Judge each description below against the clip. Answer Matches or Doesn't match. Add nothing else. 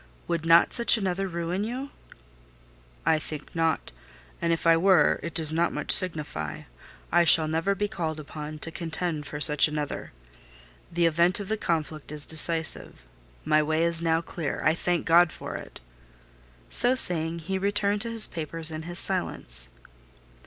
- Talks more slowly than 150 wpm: Doesn't match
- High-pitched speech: Doesn't match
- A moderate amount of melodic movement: Doesn't match